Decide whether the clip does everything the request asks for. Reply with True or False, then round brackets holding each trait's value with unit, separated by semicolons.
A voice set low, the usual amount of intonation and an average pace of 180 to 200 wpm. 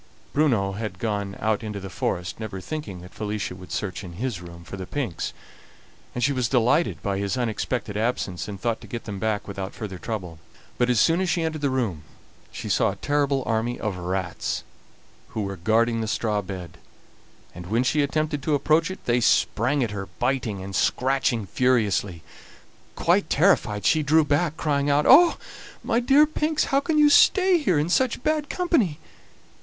False (115 Hz; 7.0 semitones; 185 wpm)